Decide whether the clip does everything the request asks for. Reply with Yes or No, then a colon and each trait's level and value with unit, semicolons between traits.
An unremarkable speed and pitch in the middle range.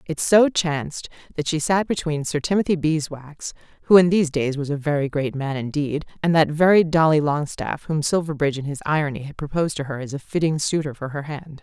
No: fast, 210 wpm; medium, 150 Hz